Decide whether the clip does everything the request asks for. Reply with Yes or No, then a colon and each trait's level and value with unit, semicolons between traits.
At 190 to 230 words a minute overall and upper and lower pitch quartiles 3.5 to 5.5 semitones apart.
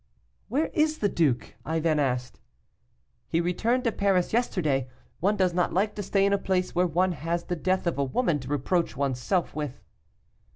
Yes: average, 195 wpm; average, 5.1 semitones